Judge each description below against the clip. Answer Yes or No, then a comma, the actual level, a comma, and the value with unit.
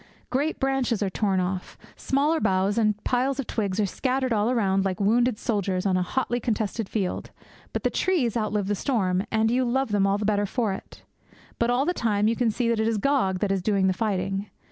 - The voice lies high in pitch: Yes, high, 215 Hz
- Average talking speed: No, fast, 220 wpm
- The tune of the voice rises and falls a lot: No, average, 3.9 semitones